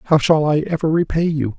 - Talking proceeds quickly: Yes, fast, 225 wpm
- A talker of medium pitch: Yes, medium, 155 Hz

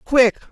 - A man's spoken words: No, female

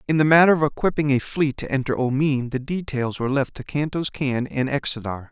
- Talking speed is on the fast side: Yes, fast, 215 wpm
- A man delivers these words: Yes, male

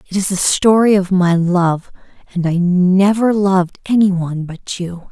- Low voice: No, medium, 185 Hz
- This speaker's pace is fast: No, average, 175 wpm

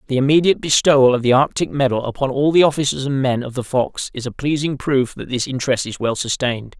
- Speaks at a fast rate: Yes, fast, 230 wpm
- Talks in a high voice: No, low, 135 Hz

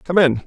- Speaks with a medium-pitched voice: Yes, medium, 165 Hz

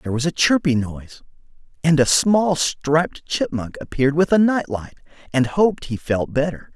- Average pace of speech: Yes, average, 180 wpm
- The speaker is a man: Yes, male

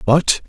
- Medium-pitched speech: Yes, medium, 145 Hz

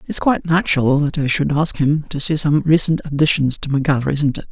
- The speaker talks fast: Yes, fast, 225 wpm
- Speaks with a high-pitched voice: No, medium, 150 Hz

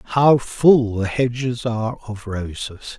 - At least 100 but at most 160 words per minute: Yes, average, 140 wpm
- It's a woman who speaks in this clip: No, male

